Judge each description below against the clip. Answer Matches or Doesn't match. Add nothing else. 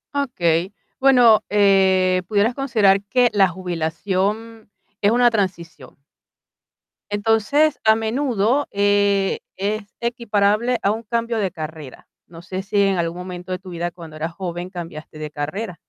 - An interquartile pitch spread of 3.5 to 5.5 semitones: Matches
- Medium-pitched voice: Doesn't match